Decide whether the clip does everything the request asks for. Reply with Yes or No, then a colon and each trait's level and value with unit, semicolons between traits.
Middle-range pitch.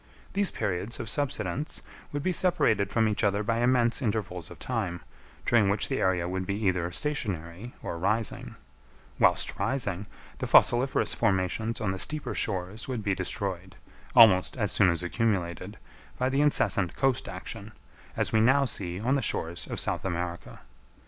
No: low, 105 Hz